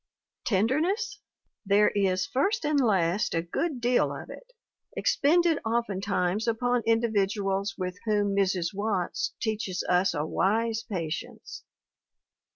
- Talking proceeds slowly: Yes, slow, 115 wpm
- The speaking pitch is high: Yes, high, 210 Hz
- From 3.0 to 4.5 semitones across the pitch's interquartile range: Yes, average, 4.1 semitones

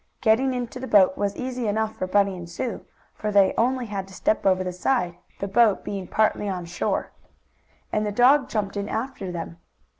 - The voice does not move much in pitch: No, average, 4.0 semitones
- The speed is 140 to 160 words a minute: No, average, 200 wpm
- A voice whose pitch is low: No, high, 205 Hz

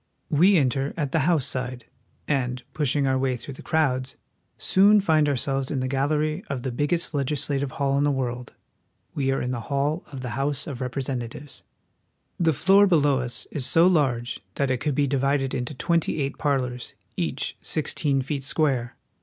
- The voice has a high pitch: No, medium, 140 Hz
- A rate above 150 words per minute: Yes, average, 180 wpm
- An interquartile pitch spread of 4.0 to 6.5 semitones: No, average, 2.7 semitones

